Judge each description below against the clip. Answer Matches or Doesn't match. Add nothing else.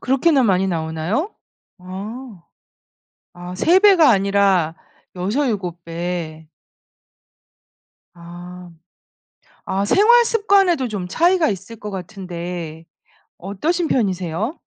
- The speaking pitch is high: Matches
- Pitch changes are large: Matches